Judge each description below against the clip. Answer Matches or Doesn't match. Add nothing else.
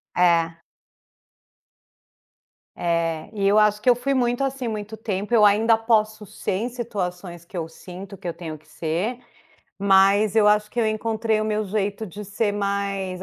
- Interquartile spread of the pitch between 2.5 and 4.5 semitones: Matches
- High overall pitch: Matches